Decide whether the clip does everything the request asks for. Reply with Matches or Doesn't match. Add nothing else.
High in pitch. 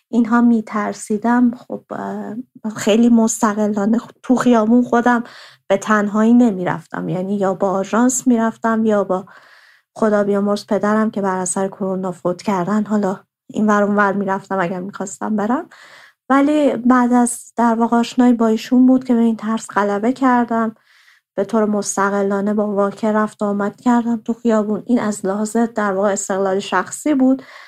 Matches